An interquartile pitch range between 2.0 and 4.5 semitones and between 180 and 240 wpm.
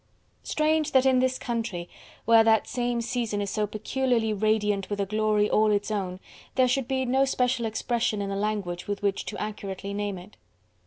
Yes: average, 3.4 semitones; average, 190 wpm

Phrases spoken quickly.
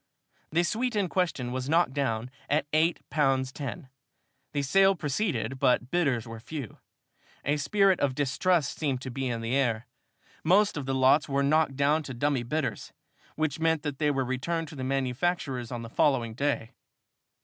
No: average, 175 wpm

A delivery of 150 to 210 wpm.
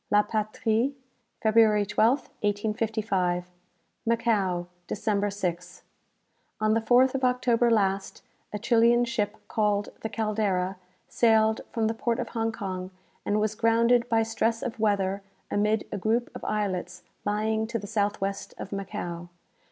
No: average, 140 wpm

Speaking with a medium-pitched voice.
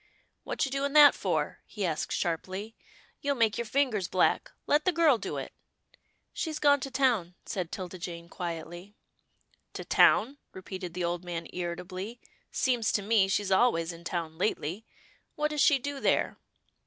No: high, 200 Hz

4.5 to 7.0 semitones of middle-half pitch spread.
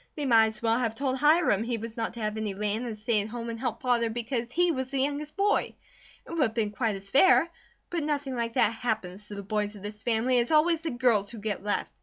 No: average, 3.7 semitones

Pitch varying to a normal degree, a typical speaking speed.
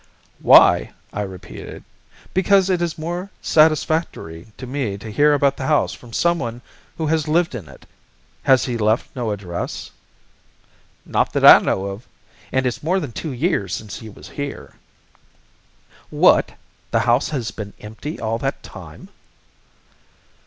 No: wide, 6.4 semitones; average, 150 wpm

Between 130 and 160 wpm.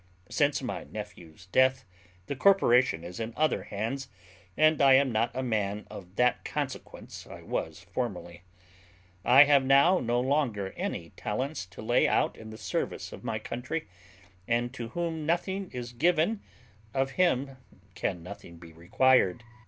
Yes: average, 150 wpm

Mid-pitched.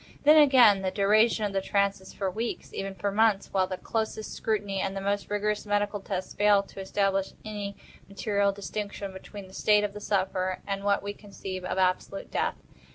No: high, 200 Hz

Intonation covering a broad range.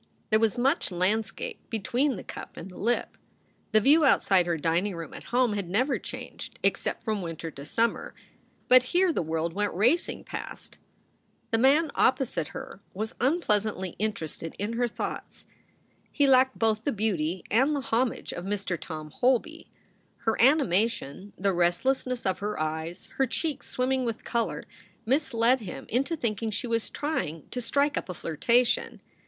Yes: wide, 5.7 semitones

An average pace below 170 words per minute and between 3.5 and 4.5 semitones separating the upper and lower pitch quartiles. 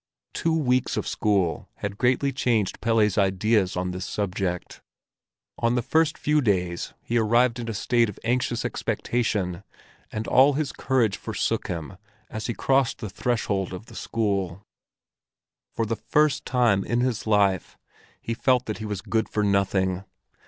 Yes: average, 160 wpm; average, 4.0 semitones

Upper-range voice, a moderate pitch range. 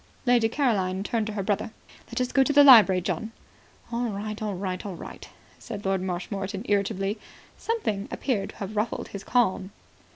Yes: high, 210 Hz; average, 3.2 semitones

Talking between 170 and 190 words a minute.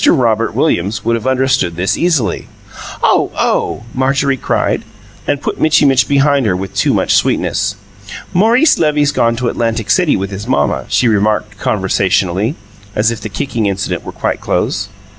No: average, 160 wpm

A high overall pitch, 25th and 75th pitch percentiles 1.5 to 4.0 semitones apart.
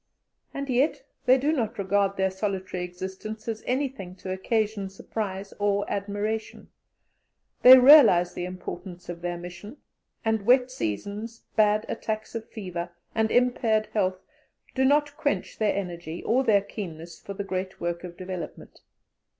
Yes: high, 205 Hz; average, 3.6 semitones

